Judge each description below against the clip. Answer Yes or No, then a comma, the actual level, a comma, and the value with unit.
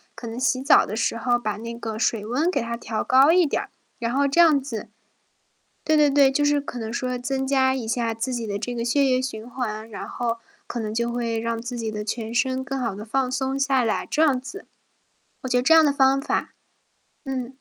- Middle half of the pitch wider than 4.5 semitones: No, average, 2.9 semitones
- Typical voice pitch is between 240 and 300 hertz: Yes, very high, 250 Hz